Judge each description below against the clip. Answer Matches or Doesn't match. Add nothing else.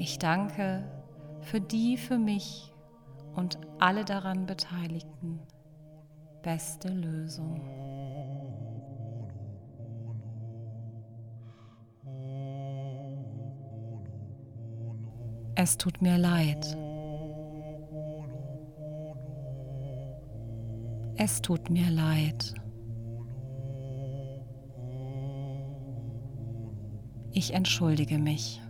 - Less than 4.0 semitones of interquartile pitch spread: Doesn't match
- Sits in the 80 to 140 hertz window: Matches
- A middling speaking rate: Doesn't match